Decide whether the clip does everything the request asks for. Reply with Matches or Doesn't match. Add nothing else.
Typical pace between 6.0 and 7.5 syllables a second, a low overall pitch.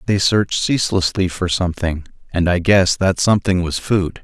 Doesn't match